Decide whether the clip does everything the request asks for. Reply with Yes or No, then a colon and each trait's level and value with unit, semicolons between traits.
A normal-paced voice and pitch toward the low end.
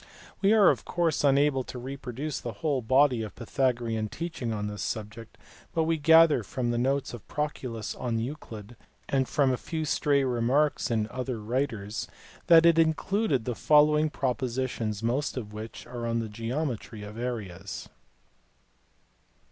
Yes: average, 155 wpm; low, 125 Hz